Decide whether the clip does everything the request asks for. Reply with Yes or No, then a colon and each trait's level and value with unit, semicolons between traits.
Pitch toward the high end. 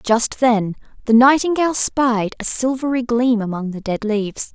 Yes: high, 235 Hz